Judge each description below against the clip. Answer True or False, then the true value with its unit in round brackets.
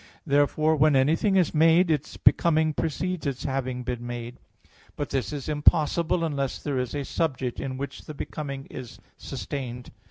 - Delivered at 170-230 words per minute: False (160 wpm)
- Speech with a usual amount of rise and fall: True (3.4 semitones)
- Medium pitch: True (145 Hz)